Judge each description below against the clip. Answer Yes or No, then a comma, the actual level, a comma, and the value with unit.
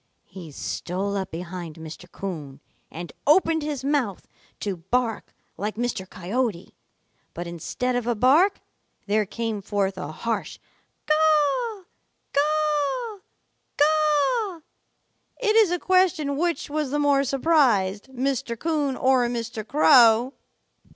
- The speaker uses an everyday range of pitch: No, wide, 7.3 semitones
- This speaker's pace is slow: Yes, slow, 120 wpm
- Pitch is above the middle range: Yes, very high, 255 Hz